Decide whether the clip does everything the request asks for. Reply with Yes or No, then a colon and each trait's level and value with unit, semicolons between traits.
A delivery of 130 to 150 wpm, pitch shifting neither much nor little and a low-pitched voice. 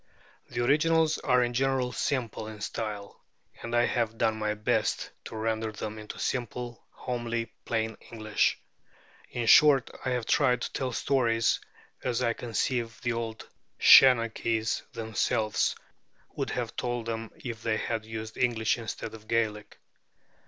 No: average, 145 wpm; narrow, 2.0 semitones; low, 115 Hz